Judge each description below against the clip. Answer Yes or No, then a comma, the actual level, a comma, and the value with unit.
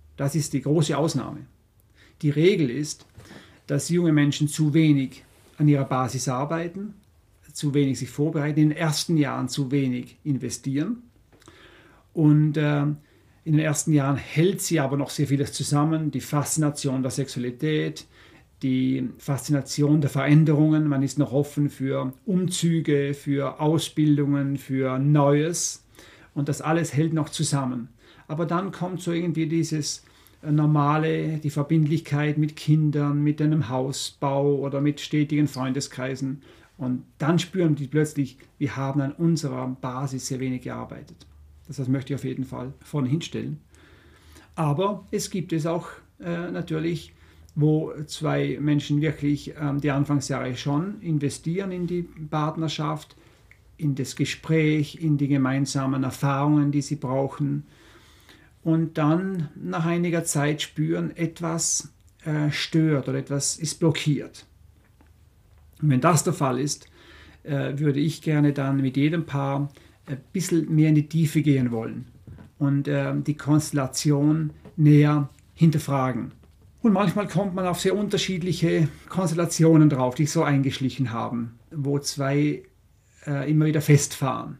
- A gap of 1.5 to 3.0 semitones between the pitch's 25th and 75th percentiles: Yes, average, 2.7 semitones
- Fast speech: No, average, 140 wpm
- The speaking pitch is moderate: Yes, medium, 145 Hz